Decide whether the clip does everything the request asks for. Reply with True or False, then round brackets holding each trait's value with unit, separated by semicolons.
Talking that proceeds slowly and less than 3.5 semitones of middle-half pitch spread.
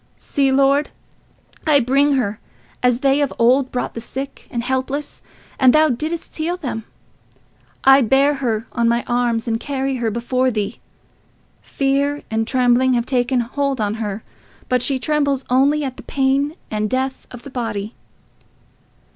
False (155 wpm; 2.8 semitones)